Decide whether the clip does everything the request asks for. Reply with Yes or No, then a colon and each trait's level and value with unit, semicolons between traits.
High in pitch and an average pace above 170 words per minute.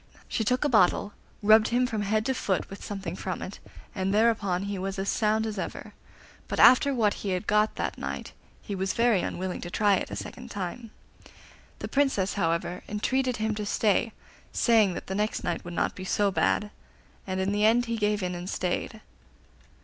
Yes: high, 205 Hz; average, 200 wpm